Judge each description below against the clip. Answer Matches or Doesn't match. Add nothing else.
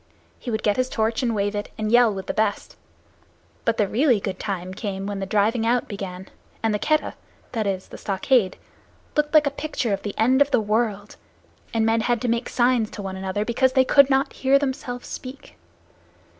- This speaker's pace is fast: Matches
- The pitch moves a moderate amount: Matches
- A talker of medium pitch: Doesn't match